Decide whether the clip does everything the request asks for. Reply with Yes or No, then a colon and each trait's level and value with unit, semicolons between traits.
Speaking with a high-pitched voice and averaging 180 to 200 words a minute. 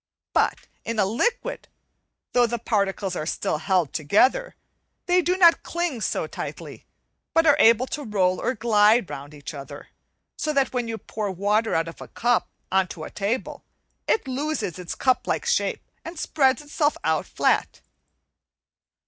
No: high, 230 Hz; average, 160 wpm